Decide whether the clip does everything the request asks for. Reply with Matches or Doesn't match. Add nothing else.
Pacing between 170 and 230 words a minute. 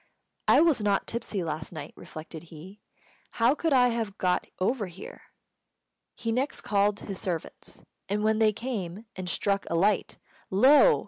Doesn't match